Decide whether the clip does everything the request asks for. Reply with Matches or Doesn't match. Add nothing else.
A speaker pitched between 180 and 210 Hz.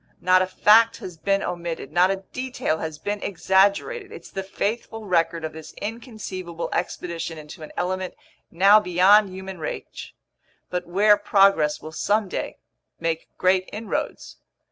Matches